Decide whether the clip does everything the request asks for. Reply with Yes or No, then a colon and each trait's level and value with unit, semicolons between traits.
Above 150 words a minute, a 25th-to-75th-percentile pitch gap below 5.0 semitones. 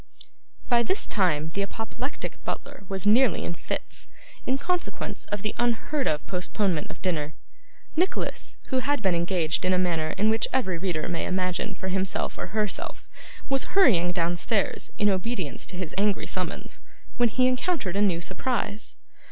No: average, 160 wpm; wide, 5.4 semitones